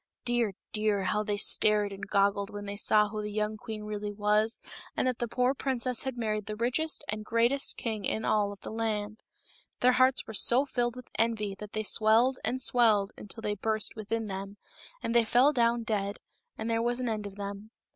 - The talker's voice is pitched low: No, high, 215 Hz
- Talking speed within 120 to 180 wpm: No, fast, 205 wpm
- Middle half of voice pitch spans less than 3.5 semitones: Yes, narrow, 2.5 semitones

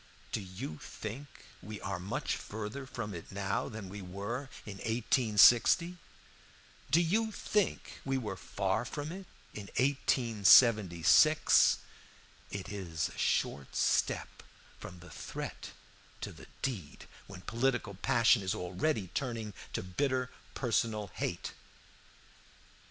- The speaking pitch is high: No, low, 110 Hz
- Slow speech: Yes, slow, 120 wpm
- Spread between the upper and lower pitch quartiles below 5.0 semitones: No, average, 5.3 semitones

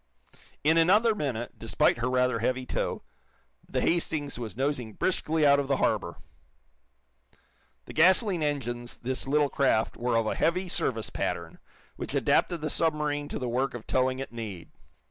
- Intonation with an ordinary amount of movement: Yes, average, 4.3 semitones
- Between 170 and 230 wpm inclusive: No, average, 160 wpm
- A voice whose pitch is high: No, low, 135 Hz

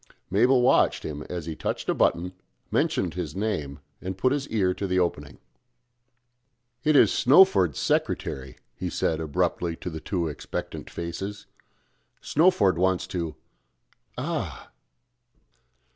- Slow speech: Yes, slow, 130 wpm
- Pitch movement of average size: Yes, average, 4.2 semitones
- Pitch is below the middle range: Yes, very low, 90 Hz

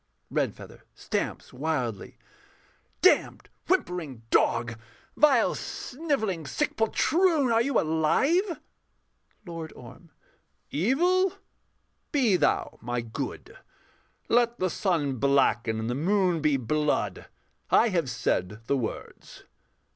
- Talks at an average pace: No, slow, 100 wpm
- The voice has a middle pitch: Yes, medium, 165 Hz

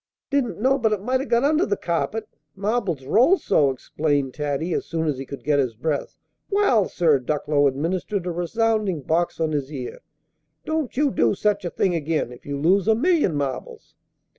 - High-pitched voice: No, medium, 175 Hz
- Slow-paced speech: No, average, 190 wpm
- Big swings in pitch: Yes, wide, 7.7 semitones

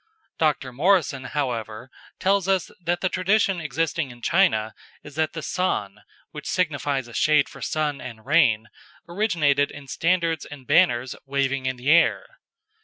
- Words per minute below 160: Yes, average, 150 wpm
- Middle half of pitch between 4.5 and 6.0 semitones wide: Yes, average, 4.9 semitones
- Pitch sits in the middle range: Yes, medium, 145 Hz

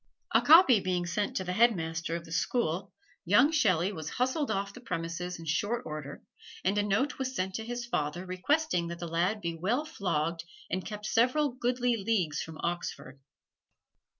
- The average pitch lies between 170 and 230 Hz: Yes, high, 190 Hz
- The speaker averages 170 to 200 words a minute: Yes, average, 180 wpm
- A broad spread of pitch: Yes, wide, 6.1 semitones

